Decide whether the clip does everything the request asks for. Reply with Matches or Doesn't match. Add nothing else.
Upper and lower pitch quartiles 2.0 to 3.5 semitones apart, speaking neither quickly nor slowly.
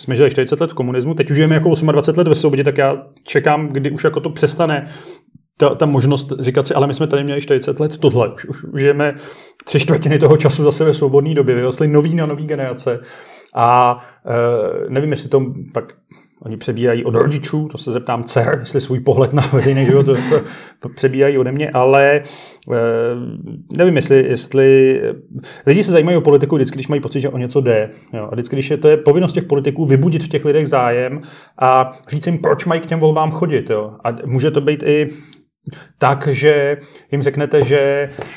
Doesn't match